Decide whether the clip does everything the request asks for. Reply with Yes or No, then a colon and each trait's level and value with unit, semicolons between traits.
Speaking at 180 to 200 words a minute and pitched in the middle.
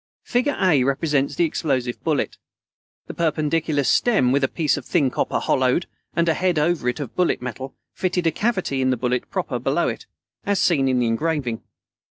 Yes: average, 190 wpm; medium, 150 Hz